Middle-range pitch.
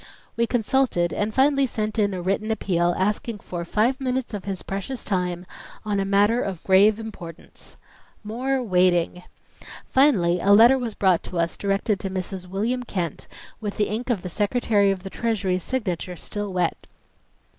No: high, 200 Hz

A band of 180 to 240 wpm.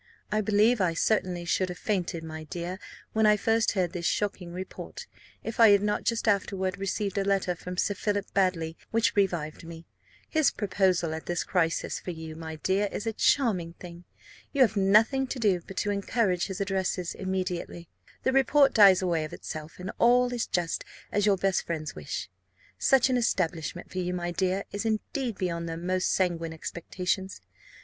Yes: average, 185 wpm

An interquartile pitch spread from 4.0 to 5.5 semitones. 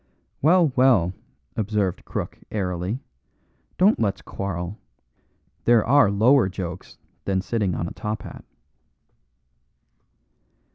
Yes: average, 4.5 semitones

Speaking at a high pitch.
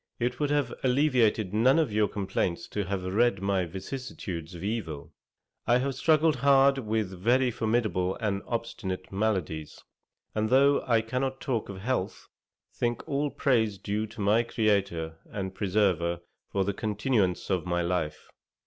No: low, 110 Hz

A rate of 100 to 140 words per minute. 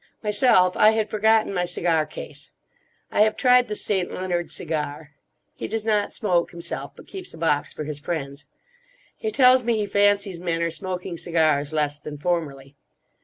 No: average, 170 wpm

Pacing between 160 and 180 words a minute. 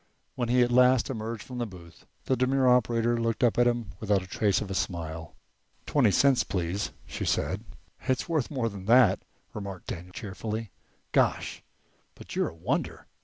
Yes: average, 175 wpm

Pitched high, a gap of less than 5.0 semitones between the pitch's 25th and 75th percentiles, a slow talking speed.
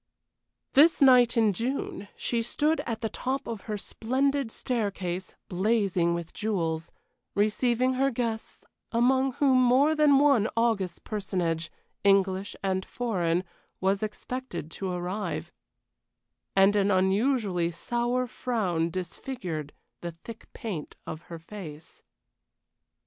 No: high, 215 Hz; wide, 5.4 semitones; slow, 115 wpm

